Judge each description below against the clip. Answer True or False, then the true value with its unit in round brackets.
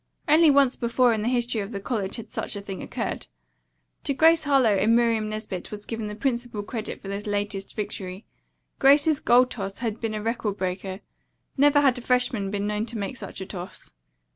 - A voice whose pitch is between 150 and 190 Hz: False (220 Hz)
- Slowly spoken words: False (200 wpm)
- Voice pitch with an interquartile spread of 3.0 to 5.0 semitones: True (3.6 semitones)